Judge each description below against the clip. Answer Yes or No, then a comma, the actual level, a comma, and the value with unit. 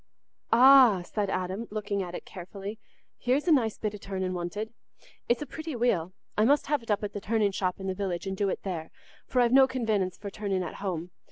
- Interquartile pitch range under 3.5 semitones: No, average, 3.9 semitones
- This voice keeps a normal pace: No, fast, 225 wpm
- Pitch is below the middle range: No, high, 205 Hz